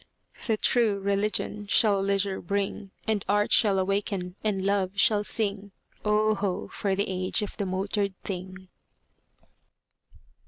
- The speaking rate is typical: No, slow, 130 wpm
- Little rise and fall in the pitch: Yes, narrow, 1.4 semitones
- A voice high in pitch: Yes, high, 200 Hz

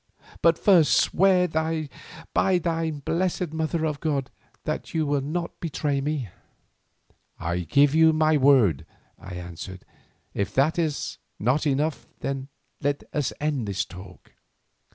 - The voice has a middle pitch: Yes, medium, 150 Hz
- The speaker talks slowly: Yes, slow, 130 wpm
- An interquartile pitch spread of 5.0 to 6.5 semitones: No, average, 3.3 semitones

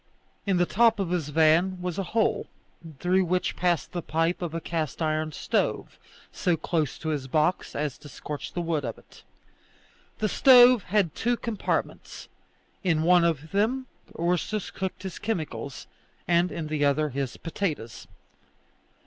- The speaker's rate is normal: Yes, average, 155 wpm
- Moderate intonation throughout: Yes, average, 3.5 semitones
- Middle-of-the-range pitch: Yes, medium, 170 Hz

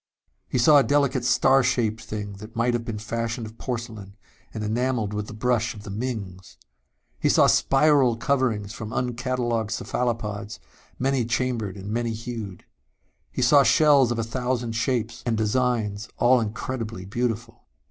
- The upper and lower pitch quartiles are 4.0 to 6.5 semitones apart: No, average, 2.7 semitones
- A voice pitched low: Yes, low, 115 Hz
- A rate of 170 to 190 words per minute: No, average, 155 wpm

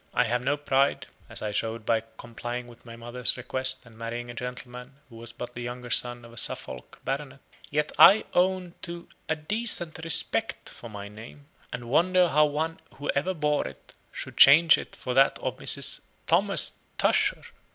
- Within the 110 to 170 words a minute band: No, average, 185 wpm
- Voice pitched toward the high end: No, low, 125 Hz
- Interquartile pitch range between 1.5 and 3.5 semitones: No, average, 4.3 semitones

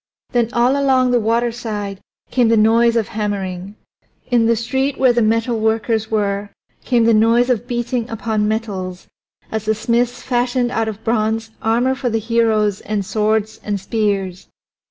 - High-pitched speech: Yes, high, 225 Hz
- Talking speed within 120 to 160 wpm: Yes, average, 155 wpm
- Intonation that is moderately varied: No, narrow, 2.1 semitones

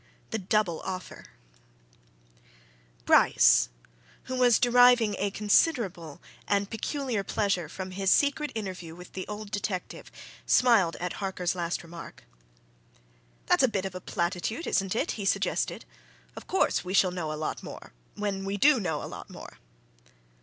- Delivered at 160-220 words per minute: No, average, 145 wpm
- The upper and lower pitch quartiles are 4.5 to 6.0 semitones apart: No, average, 3.6 semitones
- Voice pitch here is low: No, high, 195 Hz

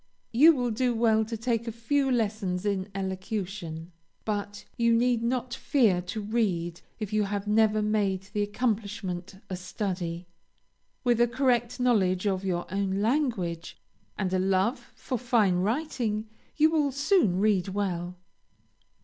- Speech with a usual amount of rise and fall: Yes, average, 4.1 semitones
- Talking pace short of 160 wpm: Yes, average, 145 wpm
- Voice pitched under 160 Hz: No, high, 210 Hz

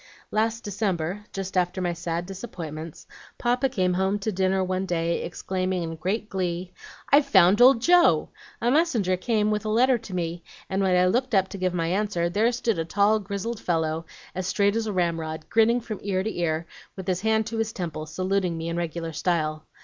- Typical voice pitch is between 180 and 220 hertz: Yes, high, 190 Hz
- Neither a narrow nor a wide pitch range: Yes, average, 4.0 semitones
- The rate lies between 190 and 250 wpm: Yes, average, 200 wpm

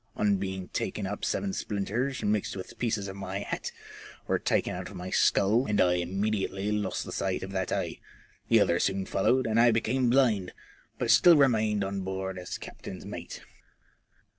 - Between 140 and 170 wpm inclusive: No, average, 180 wpm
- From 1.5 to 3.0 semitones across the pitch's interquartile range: Yes, average, 2.7 semitones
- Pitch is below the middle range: Yes, low, 100 Hz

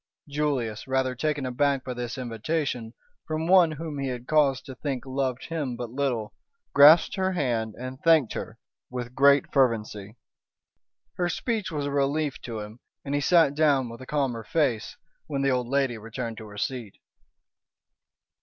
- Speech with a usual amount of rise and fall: Yes, average, 3.6 semitones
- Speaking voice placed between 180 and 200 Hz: No, low, 135 Hz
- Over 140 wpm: Yes, average, 165 wpm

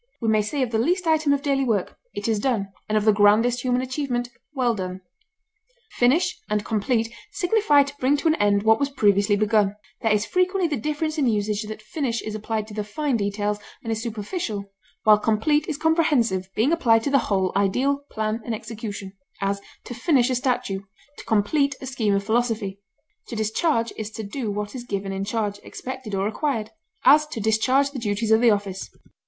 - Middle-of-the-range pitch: No, high, 225 Hz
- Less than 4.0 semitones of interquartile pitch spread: No, average, 4.7 semitones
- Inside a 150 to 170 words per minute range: No, average, 200 wpm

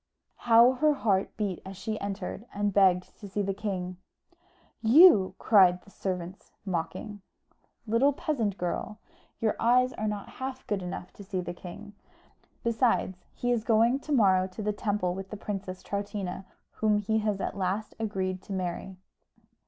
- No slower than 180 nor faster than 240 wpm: No, average, 160 wpm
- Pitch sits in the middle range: No, high, 205 Hz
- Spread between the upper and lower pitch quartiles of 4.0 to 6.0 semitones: No, average, 3.0 semitones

